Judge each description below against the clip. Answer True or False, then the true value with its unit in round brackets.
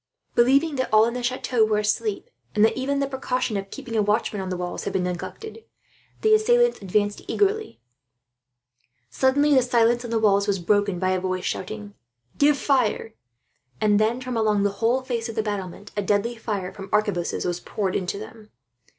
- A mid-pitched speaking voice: False (215 Hz)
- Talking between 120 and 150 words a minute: False (185 wpm)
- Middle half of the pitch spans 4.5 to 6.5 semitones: False (4.0 semitones)